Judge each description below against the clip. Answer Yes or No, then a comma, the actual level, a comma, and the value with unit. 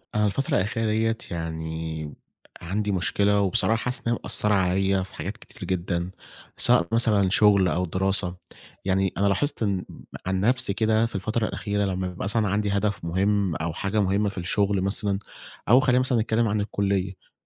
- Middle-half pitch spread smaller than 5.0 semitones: Yes, narrow, 2.5 semitones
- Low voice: Yes, low, 100 Hz